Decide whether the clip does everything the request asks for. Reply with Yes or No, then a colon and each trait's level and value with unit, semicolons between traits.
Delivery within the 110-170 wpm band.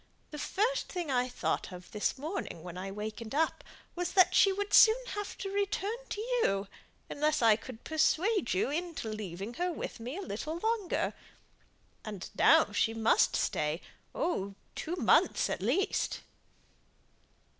Yes: average, 155 wpm